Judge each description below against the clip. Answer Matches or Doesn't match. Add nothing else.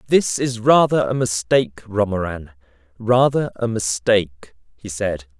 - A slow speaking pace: Matches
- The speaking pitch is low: Matches